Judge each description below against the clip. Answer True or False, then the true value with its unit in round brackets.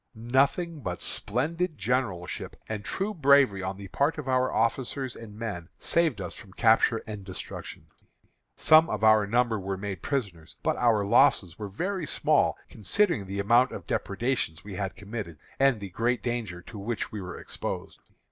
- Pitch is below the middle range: True (110 Hz)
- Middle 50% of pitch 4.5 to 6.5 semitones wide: True (5.1 semitones)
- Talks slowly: False (165 wpm)